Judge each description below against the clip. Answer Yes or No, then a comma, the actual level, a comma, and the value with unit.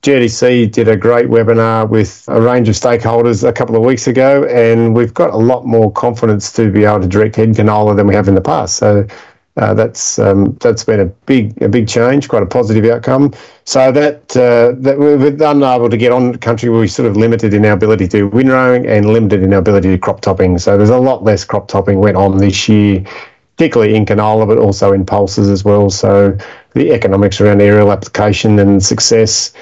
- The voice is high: No, low, 110 Hz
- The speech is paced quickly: Yes, fast, 215 wpm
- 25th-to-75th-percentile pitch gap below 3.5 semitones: Yes, average, 2.9 semitones